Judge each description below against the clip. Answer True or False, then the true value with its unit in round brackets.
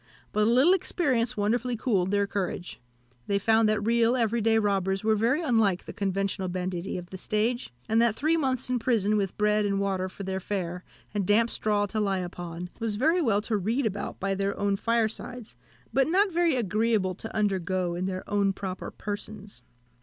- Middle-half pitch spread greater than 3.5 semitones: False (3.2 semitones)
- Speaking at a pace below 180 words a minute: False (190 wpm)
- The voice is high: True (210 Hz)